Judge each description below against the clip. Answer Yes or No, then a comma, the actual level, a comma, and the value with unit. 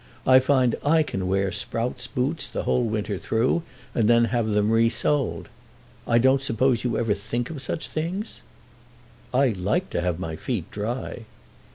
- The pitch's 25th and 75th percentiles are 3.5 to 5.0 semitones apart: Yes, average, 4.0 semitones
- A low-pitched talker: Yes, low, 120 Hz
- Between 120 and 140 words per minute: No, average, 165 wpm